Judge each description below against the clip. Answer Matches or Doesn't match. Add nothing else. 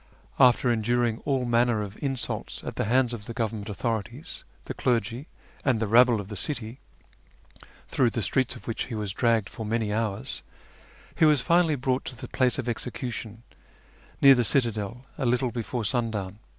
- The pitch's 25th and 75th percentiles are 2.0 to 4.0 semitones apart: Matches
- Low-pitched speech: Matches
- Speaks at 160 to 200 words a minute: Matches